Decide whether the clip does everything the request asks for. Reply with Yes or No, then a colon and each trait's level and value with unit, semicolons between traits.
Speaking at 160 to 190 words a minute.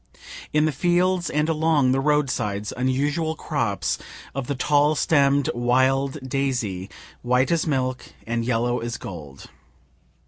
No: slow, 135 wpm